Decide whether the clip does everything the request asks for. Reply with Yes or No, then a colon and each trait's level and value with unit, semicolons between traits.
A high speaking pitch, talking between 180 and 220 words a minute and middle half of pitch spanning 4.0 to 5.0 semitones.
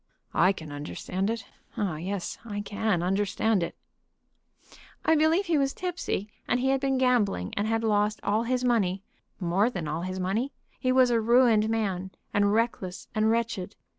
No: high, 215 Hz; average, 170 wpm; average, 4.4 semitones